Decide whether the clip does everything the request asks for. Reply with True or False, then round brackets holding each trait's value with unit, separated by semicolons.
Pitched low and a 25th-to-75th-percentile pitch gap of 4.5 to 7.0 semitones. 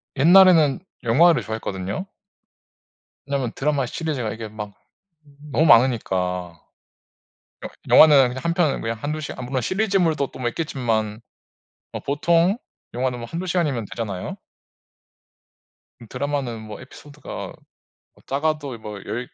True (130 Hz; 5.4 semitones)